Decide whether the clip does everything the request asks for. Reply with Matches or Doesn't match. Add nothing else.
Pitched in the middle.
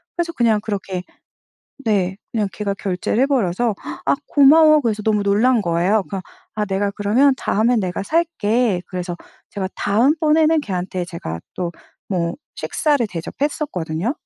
Doesn't match